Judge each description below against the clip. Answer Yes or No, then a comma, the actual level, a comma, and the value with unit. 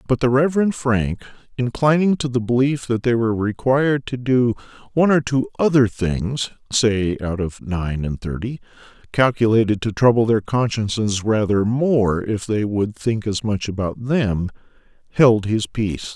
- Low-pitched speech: Yes, low, 115 Hz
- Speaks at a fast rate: No, average, 160 wpm